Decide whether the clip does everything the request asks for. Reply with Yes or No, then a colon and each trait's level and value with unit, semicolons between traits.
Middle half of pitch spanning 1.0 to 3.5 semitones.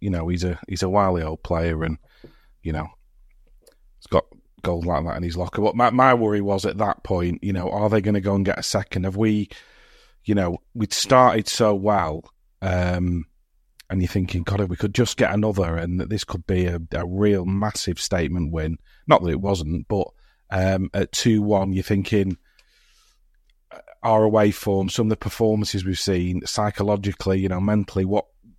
Yes: average, 2.9 semitones